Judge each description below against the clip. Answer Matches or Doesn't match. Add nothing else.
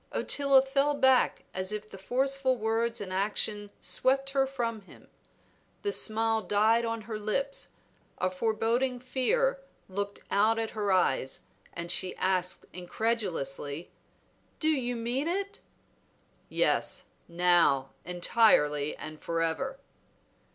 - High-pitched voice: Matches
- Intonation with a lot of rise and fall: Matches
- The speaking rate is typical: Doesn't match